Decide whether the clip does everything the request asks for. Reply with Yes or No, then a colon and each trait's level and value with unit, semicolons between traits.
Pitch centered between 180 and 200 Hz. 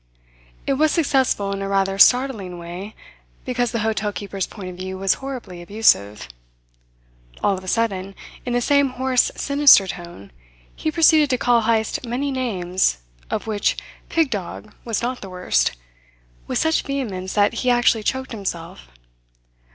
No: high, 220 Hz